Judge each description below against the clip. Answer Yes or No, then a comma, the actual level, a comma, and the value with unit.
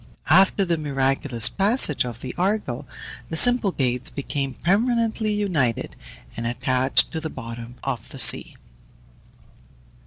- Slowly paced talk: Yes, slow, 120 wpm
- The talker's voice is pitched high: No, medium, 145 Hz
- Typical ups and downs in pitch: No, wide, 7.7 semitones